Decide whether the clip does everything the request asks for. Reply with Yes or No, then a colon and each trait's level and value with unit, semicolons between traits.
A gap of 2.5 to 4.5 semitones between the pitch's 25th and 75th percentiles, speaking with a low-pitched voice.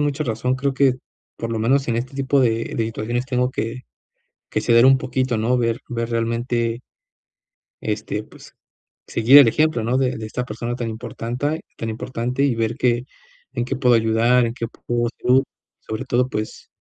No: narrow, 2.1 semitones; low, 120 Hz